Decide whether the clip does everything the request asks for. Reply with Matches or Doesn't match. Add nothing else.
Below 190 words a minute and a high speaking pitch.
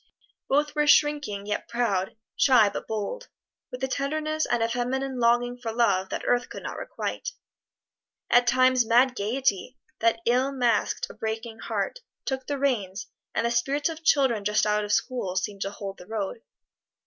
Matches